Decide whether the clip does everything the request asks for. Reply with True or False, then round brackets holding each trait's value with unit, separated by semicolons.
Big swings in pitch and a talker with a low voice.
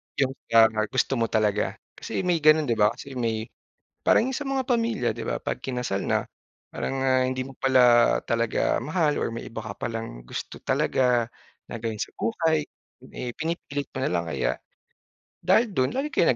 True (5.8 semitones; 130 Hz)